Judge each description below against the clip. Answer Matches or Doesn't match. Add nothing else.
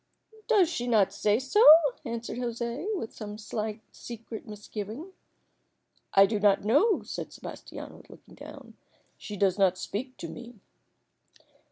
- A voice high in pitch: Matches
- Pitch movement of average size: Matches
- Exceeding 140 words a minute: Doesn't match